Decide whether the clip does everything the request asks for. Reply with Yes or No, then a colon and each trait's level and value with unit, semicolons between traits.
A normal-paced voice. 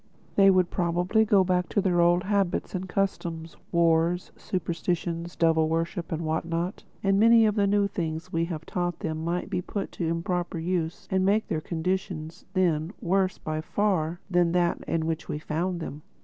Yes: average, 180 wpm